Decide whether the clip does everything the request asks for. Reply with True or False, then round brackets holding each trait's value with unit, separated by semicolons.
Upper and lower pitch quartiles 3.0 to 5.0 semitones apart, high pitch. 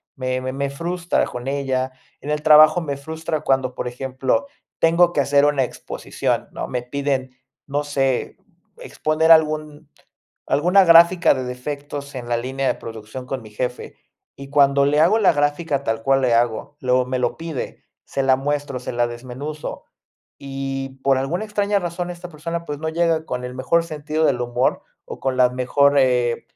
False (3.4 semitones; 140 Hz)